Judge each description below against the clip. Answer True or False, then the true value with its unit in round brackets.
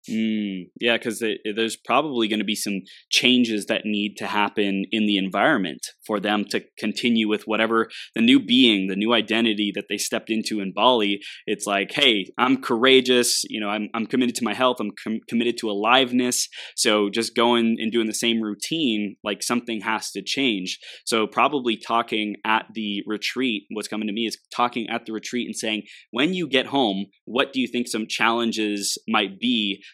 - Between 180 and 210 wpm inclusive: True (190 wpm)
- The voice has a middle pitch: False (110 Hz)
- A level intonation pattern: True (2.2 semitones)